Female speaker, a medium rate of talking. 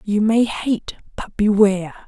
Yes: female; average, 145 wpm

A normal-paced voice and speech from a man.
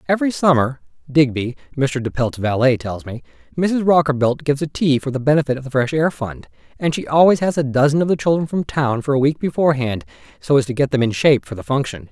No: fast, 235 wpm; male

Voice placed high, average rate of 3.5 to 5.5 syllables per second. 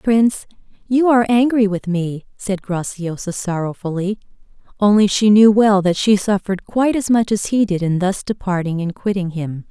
Yes: high, 200 Hz; 5.0 syllables/s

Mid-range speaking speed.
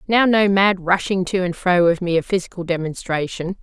Yes: average, 180 wpm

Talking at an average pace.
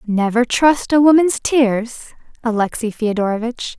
No: slow, 110 wpm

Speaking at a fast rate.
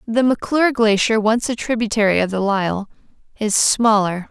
No: average, 155 wpm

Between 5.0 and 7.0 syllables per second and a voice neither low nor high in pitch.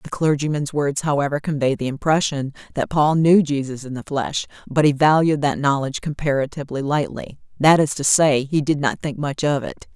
Yes: 5.4 syllables/s; medium, 145 Hz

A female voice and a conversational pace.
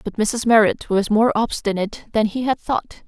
Yes: female; average, 195 wpm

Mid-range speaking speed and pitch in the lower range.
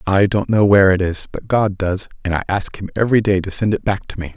No: fast, 290 wpm; very low, 95 Hz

